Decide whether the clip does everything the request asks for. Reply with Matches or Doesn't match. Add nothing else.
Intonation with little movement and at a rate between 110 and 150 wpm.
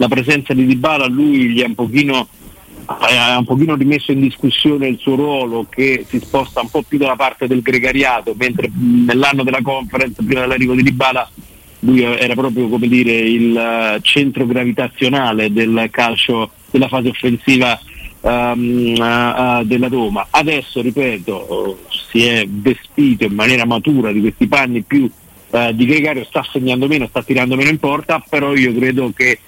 Doesn't match